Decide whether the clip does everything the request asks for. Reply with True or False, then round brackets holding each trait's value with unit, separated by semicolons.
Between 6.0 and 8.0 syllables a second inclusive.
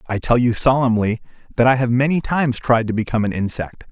True (6.4 syllables/s)